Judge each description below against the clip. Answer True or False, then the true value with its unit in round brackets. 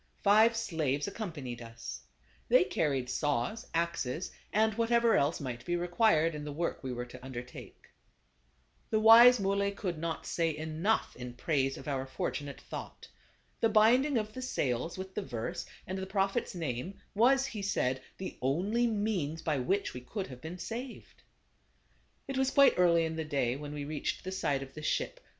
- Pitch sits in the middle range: True (170 Hz)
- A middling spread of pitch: False (7.4 semitones)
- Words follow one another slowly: False (175 wpm)